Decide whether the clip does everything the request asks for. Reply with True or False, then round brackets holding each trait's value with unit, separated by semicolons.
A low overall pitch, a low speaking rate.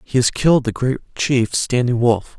False (125 Hz; 200 wpm)